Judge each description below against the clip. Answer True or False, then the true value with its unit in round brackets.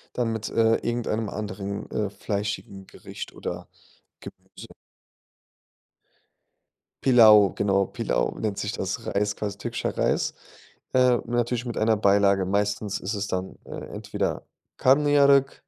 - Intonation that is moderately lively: True (3.0 semitones)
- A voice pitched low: True (105 Hz)